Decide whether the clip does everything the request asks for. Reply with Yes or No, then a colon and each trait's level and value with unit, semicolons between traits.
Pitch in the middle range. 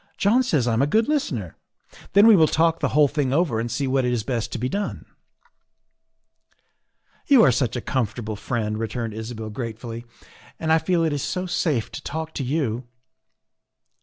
No: low, 130 Hz